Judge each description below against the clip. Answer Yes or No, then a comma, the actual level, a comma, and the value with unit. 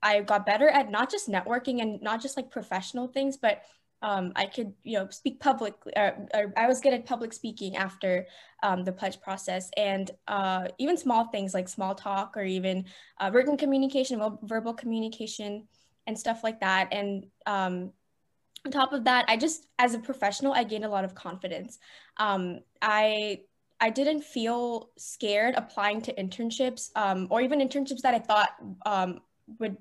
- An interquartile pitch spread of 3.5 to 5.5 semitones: Yes, average, 4.0 semitones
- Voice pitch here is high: Yes, high, 215 Hz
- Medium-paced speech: Yes, average, 175 wpm